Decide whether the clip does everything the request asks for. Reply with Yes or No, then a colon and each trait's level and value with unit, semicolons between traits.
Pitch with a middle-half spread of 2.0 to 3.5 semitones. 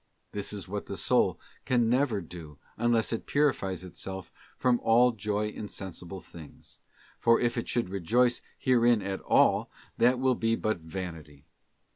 No: average, 4.3 semitones